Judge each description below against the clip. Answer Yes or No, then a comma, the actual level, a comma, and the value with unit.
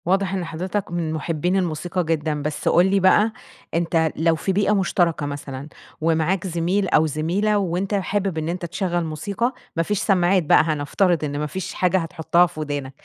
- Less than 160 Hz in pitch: No, medium, 170 Hz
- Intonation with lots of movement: No, average, 3.3 semitones